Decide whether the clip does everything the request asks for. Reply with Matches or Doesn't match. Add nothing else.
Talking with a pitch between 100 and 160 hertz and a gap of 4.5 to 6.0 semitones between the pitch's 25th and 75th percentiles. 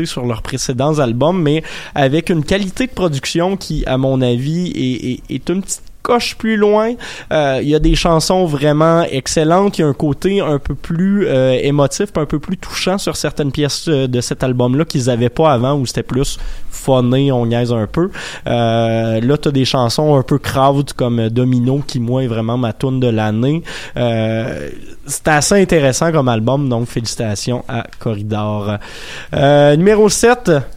Matches